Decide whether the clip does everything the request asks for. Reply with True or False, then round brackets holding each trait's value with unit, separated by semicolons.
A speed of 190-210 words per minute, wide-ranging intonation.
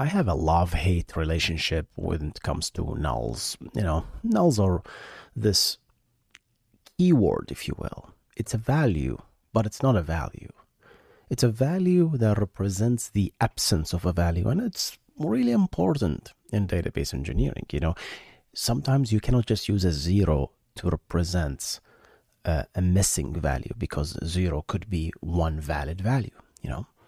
False (150 wpm; 6.2 semitones)